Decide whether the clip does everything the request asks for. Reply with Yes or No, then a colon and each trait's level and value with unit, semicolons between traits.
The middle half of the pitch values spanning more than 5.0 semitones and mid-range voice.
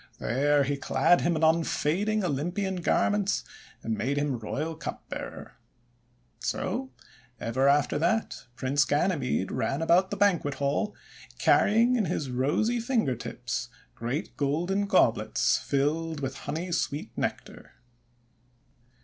Yes: wide, 5.4 semitones; medium, 155 Hz